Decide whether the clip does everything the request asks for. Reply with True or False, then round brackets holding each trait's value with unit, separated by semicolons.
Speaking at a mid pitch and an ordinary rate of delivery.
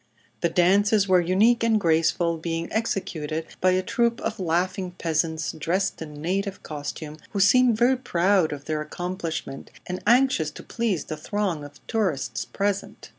True (180 Hz; 155 wpm)